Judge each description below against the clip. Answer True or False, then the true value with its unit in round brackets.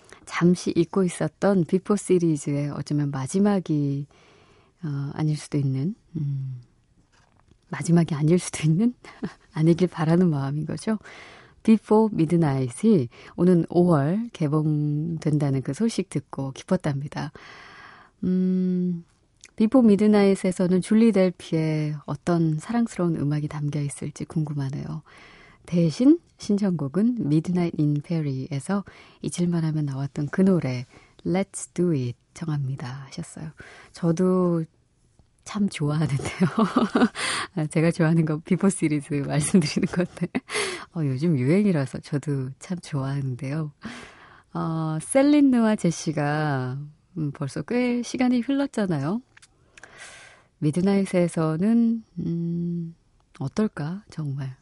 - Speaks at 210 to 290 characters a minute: True (250 characters per minute)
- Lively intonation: False (4.5 semitones)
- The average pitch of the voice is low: False (165 Hz)